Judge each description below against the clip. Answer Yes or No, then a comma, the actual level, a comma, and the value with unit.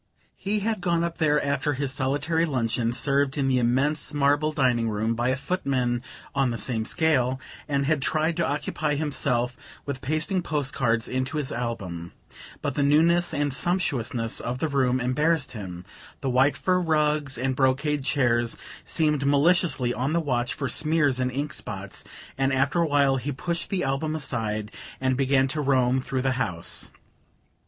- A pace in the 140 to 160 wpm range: No, average, 170 wpm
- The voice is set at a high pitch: No, low, 135 Hz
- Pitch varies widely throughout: No, average, 3.3 semitones